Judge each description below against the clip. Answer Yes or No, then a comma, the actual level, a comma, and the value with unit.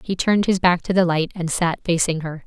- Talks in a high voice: No, medium, 175 Hz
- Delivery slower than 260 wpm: No, fast, 270 wpm